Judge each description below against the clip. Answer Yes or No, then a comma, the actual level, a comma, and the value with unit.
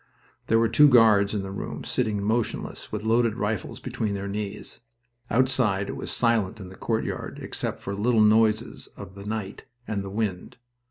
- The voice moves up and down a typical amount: No, narrow, 2.3 semitones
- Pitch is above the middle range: No, low, 105 Hz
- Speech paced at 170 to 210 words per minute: Yes, average, 175 wpm